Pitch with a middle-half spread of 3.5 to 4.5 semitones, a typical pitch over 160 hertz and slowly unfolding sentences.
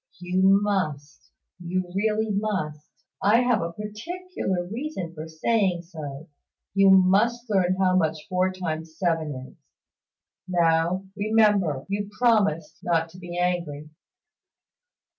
Yes: average, 4.0 semitones; medium, 185 Hz; slow, 120 wpm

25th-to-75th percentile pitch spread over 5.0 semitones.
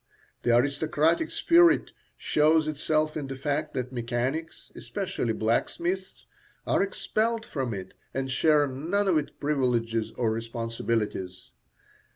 Yes: wide, 5.4 semitones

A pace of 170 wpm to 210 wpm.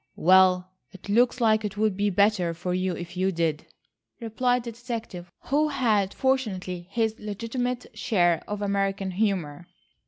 No: average, 150 wpm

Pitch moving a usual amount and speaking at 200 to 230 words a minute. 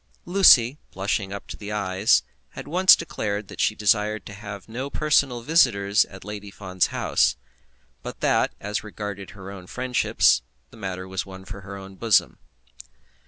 No: average, 3.2 semitones; average, 165 wpm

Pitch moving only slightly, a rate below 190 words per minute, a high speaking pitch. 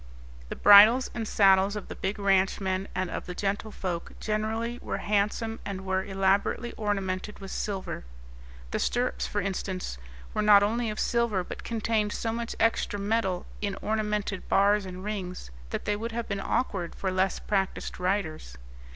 Yes: narrow, 2.2 semitones; average, 160 wpm; high, 205 Hz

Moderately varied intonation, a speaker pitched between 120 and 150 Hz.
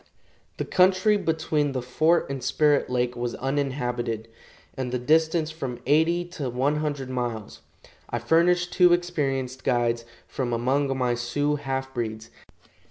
Yes: average, 4.4 semitones; low, 135 Hz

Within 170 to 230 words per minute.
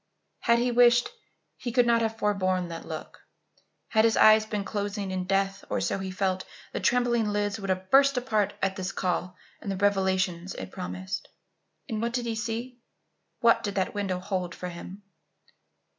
Yes: average, 180 wpm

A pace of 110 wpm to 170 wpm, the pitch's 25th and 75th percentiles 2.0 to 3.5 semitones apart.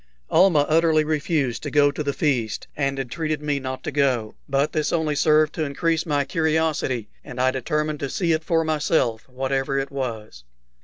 No: average, 185 wpm; average, 2.9 semitones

